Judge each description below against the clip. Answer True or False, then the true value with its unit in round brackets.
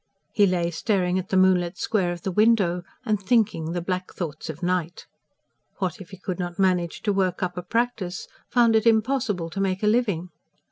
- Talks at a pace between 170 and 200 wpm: True (195 wpm)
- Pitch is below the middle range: False (185 Hz)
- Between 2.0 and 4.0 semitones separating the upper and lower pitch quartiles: True (3.1 semitones)